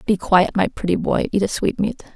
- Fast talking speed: Yes, fast, 225 wpm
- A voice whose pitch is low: No, high, 195 Hz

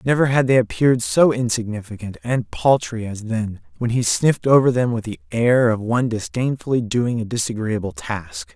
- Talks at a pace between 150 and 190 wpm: Yes, average, 175 wpm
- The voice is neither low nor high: No, low, 115 Hz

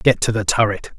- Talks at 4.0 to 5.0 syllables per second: No, 5.6 syllables/s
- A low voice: Yes, low, 110 Hz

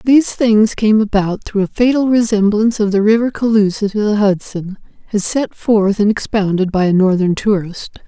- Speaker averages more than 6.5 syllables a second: No, 5.1 syllables/s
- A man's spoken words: No, female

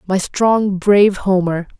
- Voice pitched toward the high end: Yes, high, 195 Hz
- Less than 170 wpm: Yes, slow, 135 wpm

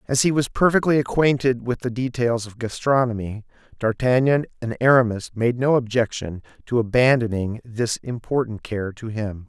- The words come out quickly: No, average, 145 wpm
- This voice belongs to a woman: No, male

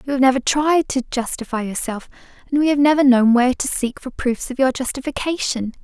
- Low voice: No, very high, 260 Hz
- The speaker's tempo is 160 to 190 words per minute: No, fast, 205 wpm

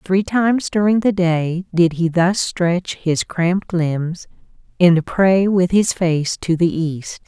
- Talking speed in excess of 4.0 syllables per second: No, 3.5 syllables/s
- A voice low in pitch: No, medium, 180 Hz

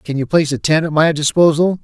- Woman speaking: No, male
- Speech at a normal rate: No, fast, 260 wpm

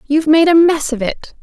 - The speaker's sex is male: No, female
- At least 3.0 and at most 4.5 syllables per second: No, 6.7 syllables/s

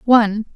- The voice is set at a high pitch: Yes, high, 220 Hz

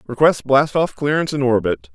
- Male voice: Yes, male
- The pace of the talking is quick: No, average, 185 wpm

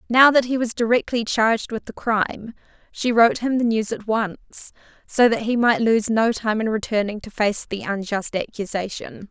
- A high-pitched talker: Yes, high, 225 Hz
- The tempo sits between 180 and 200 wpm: Yes, average, 195 wpm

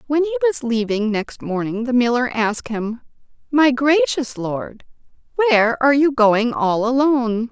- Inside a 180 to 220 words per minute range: No, average, 150 wpm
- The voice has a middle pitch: No, very high, 250 Hz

